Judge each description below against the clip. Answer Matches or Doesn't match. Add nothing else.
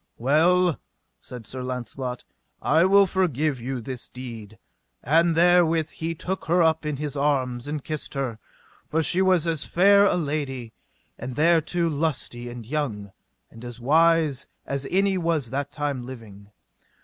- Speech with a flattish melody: Doesn't match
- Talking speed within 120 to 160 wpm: Matches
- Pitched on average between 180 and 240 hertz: Doesn't match